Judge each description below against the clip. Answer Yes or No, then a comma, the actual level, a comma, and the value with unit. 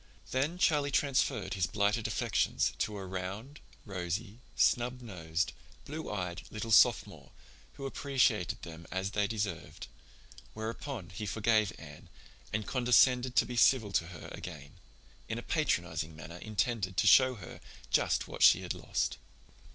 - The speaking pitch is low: Yes, low, 105 Hz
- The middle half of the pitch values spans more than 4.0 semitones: Yes, average, 5.3 semitones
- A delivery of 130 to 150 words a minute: Yes, average, 145 wpm